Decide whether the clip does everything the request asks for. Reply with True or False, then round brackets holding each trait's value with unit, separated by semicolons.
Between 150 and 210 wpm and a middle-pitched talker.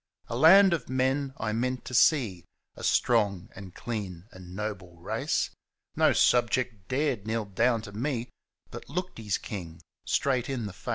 False (170 wpm; 115 Hz)